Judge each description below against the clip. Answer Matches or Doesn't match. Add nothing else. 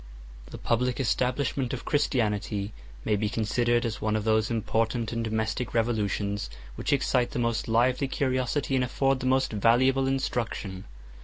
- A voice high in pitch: Doesn't match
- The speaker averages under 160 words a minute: Matches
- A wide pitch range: Doesn't match